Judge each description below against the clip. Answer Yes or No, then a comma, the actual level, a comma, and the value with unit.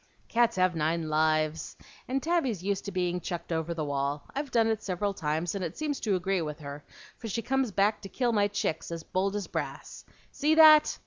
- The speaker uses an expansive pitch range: Yes, wide, 6.1 semitones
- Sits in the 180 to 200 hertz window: Yes, high, 190 Hz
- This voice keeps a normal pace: No, fast, 210 wpm